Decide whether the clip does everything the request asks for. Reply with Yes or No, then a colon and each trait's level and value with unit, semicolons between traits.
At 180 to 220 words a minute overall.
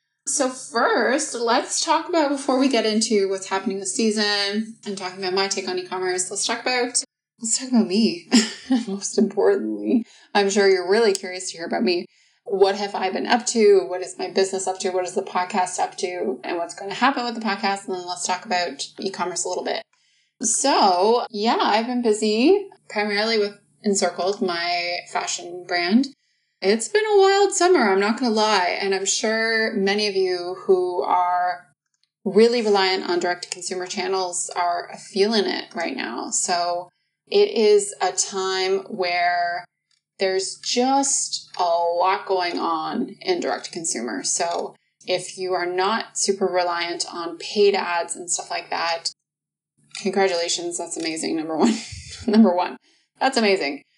No: average, 170 wpm